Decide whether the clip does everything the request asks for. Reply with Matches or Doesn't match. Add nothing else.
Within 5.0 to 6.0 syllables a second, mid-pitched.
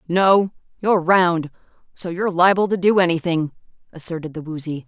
Matches